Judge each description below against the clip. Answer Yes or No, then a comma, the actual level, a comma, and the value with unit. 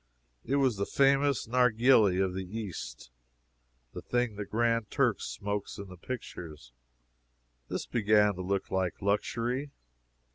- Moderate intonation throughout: Yes, average, 4.3 semitones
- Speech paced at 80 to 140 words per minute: Yes, slow, 135 wpm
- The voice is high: No, low, 105 Hz